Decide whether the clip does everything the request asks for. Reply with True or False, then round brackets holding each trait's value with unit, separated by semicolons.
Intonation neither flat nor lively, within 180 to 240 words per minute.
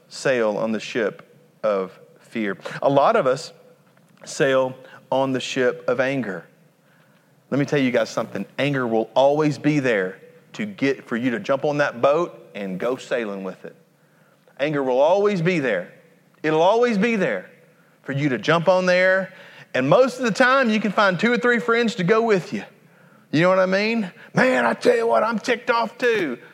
False (7.1 semitones; 195 wpm)